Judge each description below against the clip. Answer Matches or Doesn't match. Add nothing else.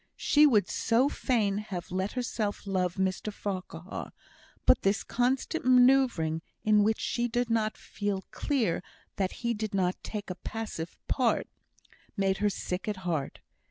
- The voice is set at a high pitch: Matches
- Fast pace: Doesn't match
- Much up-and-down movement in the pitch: Doesn't match